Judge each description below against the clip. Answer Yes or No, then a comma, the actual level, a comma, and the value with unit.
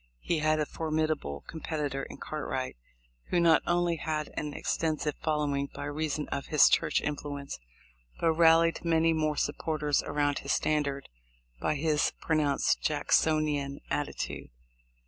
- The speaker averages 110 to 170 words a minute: Yes, slow, 135 wpm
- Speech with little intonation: Yes, narrow, 1.7 semitones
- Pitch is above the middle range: No, medium, 150 Hz